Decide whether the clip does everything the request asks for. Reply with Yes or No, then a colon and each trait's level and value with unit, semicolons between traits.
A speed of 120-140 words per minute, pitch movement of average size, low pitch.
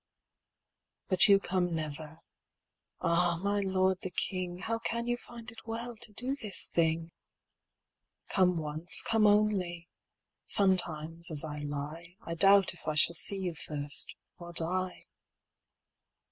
No: slow, 135 wpm; average, 3.6 semitones; medium, 180 Hz